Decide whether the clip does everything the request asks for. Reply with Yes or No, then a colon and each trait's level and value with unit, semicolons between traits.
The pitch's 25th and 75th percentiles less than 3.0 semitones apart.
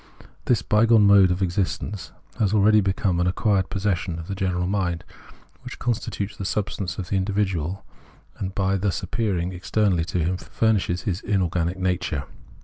Yes: narrow, 2.4 semitones